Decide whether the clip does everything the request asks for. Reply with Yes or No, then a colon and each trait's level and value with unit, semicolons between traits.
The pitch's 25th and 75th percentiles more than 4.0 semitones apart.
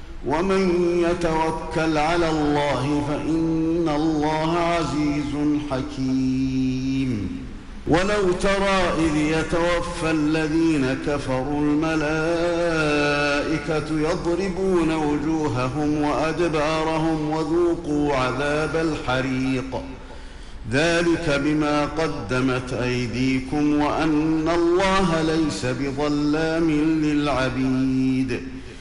No: average, 2.7 semitones